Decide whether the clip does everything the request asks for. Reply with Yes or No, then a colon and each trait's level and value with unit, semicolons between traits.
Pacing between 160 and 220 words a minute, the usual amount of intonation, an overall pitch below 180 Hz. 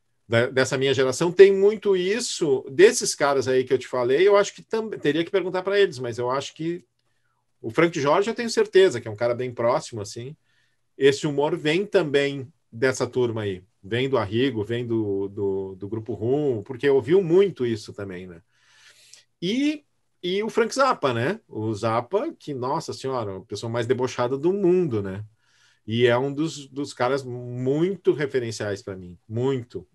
No: average, 180 wpm; wide, 7.7 semitones; low, 135 Hz